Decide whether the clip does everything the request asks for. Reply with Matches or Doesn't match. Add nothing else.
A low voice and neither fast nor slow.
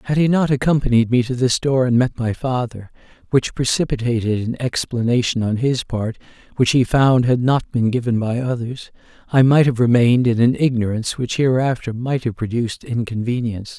Matches